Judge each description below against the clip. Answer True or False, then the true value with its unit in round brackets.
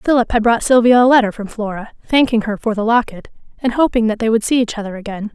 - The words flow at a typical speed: False (245 wpm)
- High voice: True (225 Hz)